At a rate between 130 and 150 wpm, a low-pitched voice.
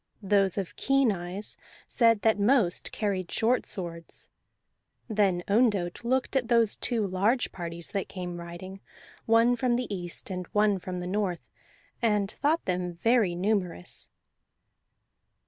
No: slow, 135 wpm; high, 200 Hz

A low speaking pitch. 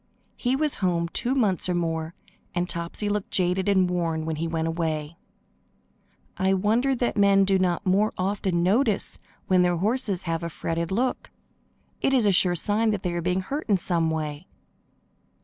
No: medium, 185 Hz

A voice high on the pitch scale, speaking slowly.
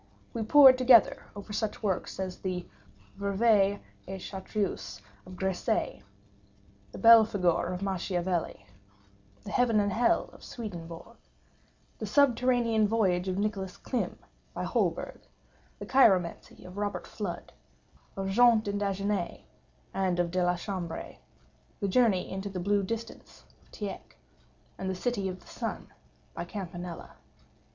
Yes: high, 200 Hz; slow, 130 wpm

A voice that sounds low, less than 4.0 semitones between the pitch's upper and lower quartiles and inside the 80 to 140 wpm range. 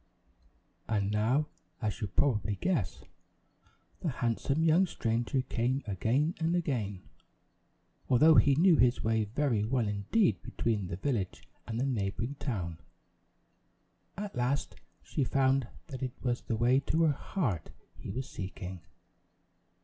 No: low, 120 Hz; average, 5.1 semitones; slow, 135 wpm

